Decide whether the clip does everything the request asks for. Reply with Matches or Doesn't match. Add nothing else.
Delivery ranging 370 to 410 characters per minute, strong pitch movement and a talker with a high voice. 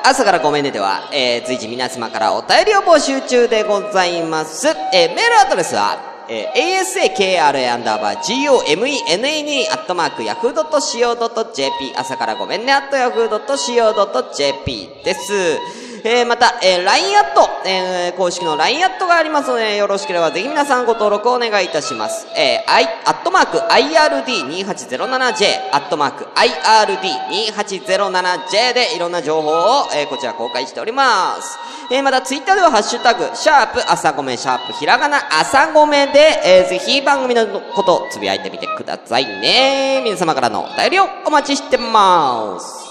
Matches